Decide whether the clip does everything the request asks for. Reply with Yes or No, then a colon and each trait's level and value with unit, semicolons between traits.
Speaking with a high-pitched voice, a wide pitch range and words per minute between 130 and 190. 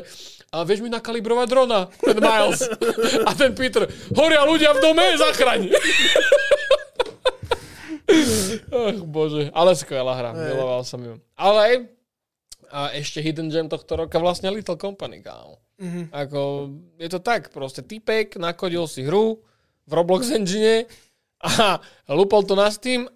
Yes: high, 200 Hz; wide, 7.5 semitones; average, 135 wpm